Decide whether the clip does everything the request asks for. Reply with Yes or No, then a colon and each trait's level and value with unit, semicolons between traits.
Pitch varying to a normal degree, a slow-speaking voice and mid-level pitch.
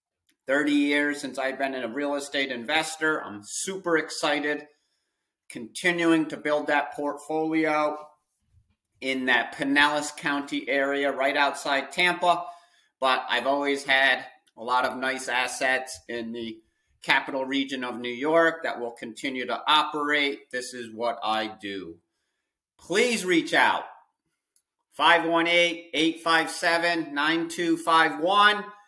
Yes: average, 3.8 semitones; slow, 120 wpm; medium, 145 Hz